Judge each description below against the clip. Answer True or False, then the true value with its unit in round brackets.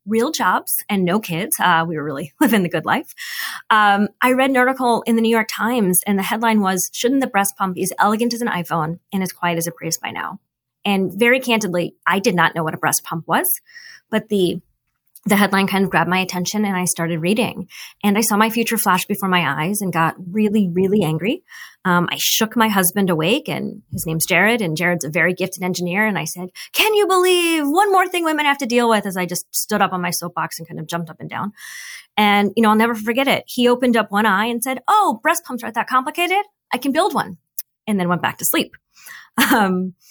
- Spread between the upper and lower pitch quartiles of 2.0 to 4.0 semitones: False (5.2 semitones)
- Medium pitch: False (205 Hz)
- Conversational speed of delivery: False (240 wpm)